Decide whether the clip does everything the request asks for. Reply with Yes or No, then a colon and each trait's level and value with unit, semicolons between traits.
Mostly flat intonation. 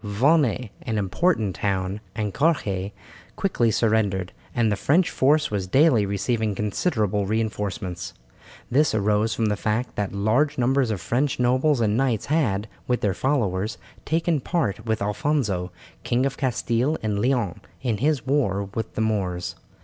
No: average, 4.8 semitones